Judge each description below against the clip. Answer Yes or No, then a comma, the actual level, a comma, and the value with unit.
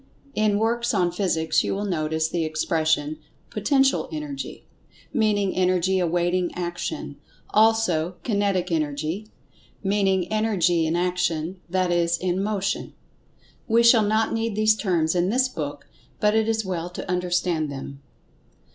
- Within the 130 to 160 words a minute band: Yes, slow, 135 wpm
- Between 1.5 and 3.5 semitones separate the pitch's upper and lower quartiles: No, average, 4.3 semitones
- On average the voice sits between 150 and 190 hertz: Yes, medium, 185 Hz